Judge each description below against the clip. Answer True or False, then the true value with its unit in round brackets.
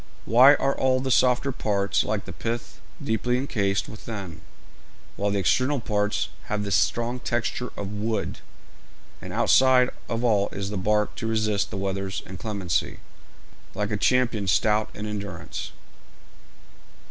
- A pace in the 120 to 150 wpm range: True (140 wpm)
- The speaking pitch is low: True (105 Hz)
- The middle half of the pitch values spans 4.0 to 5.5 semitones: False (3.4 semitones)